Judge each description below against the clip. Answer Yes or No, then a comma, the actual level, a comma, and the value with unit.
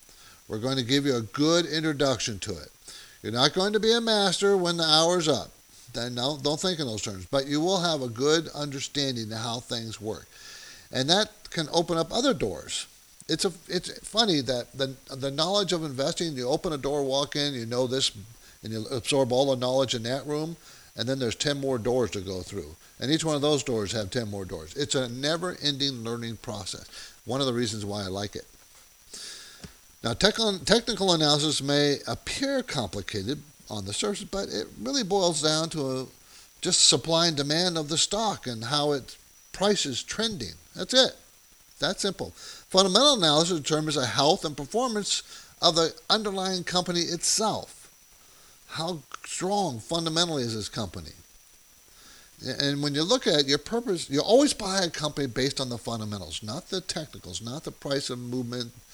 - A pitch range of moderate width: No, wide, 5.9 semitones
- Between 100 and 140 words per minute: No, average, 185 wpm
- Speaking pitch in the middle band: Yes, medium, 145 Hz